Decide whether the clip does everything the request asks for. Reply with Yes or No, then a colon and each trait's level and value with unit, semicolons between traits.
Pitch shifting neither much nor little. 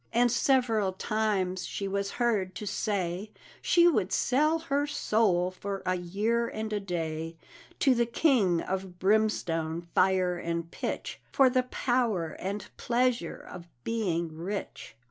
Yes: average, 4.8 semitones